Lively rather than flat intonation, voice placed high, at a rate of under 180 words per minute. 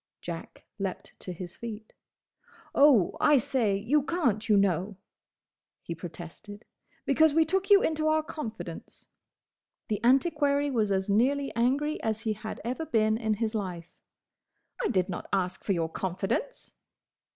Yes: wide, 6.6 semitones; high, 220 Hz; average, 145 wpm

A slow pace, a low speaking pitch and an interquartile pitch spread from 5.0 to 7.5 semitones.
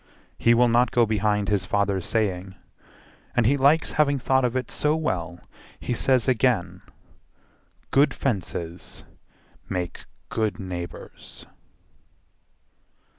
Yes: slow, 115 wpm; low, 110 Hz; wide, 5.4 semitones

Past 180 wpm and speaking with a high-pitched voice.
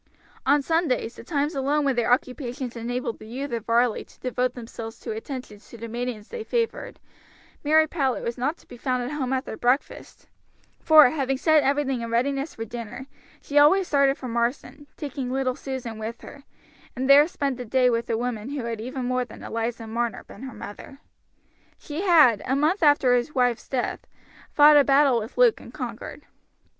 Yes: average, 190 wpm; very high, 255 Hz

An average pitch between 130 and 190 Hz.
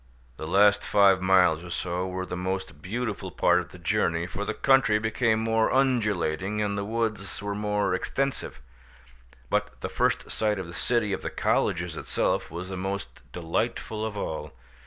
No: low, 100 Hz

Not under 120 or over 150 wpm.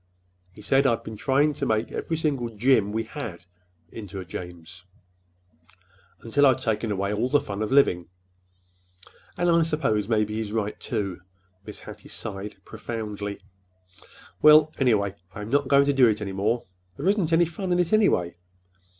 No: average, 165 wpm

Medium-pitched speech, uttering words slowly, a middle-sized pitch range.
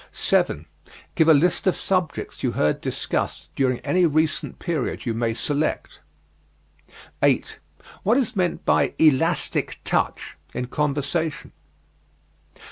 Yes: medium, 155 Hz; slow, 120 wpm; average, 5.0 semitones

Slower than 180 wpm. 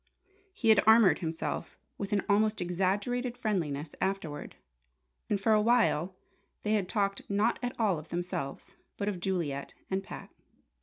Yes: average, 150 wpm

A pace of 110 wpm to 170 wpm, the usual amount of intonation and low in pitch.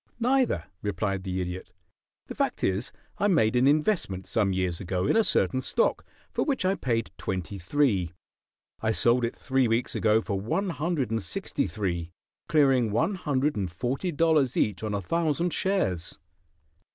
No: average, 165 wpm; wide, 8.4 semitones; low, 115 Hz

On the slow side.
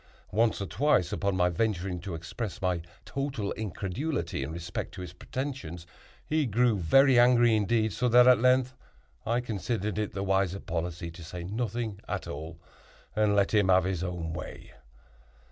No: average, 165 wpm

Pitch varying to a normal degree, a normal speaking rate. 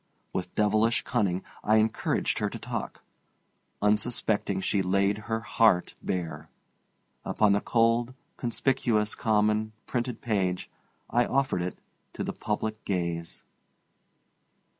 No: average, 3.2 semitones; slow, 115 wpm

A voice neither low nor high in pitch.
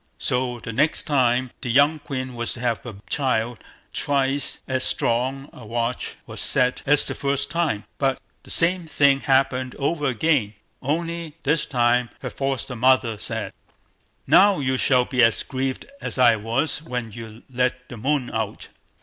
No: low, 130 Hz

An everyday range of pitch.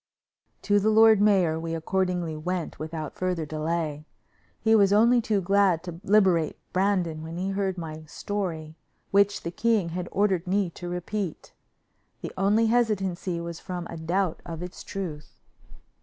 Yes: average, 3.5 semitones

